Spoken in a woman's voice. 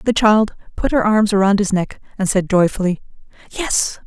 Yes: female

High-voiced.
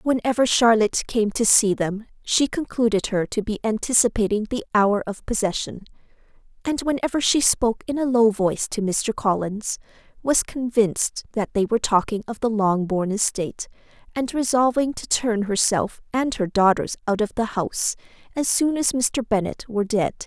Yes: high, 225 Hz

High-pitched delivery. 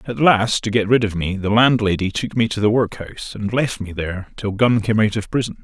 No: low, 110 Hz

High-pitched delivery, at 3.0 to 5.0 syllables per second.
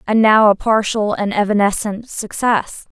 Yes: high, 210 Hz; 4.4 syllables/s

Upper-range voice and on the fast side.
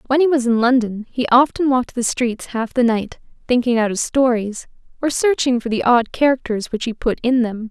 Yes: high, 245 Hz; fast, 220 wpm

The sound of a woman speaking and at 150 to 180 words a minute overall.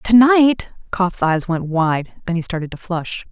No: female; average, 200 wpm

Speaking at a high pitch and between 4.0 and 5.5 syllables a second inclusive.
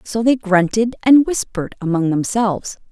Yes: high, 210 Hz; 5.0 syllables/s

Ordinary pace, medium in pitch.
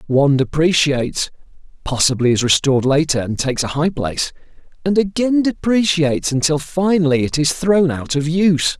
Yes: average, 150 wpm; medium, 155 Hz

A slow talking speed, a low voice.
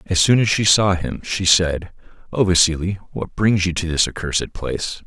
No: average, 200 wpm; very low, 90 Hz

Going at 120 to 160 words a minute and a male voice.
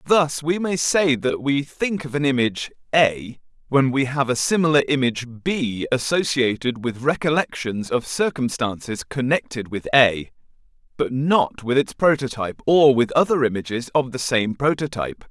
Yes: average, 155 wpm; male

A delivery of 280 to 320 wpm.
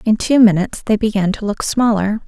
No: fast, 210 wpm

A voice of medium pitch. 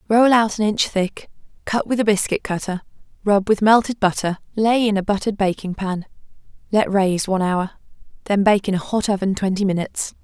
No: high, 200 Hz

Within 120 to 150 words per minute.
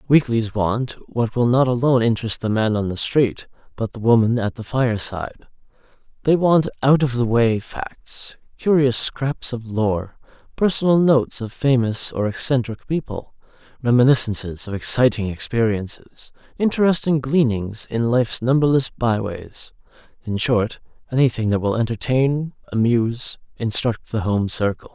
Yes: average, 140 wpm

